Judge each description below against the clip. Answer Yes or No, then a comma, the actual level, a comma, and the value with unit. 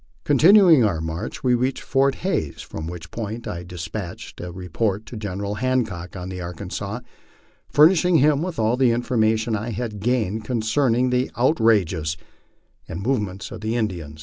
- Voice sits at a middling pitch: No, low, 110 Hz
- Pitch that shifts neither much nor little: No, wide, 5.8 semitones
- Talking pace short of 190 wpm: Yes, average, 160 wpm